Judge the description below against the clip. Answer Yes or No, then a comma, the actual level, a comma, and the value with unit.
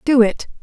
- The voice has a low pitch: No, high, 245 Hz